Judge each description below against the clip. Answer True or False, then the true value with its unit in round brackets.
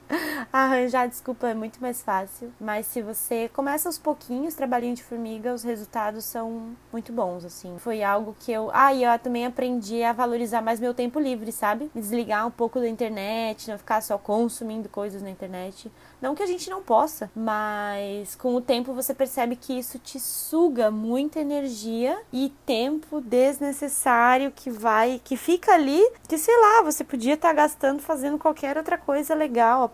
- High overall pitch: True (245 Hz)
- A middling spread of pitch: True (3.9 semitones)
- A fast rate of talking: False (175 wpm)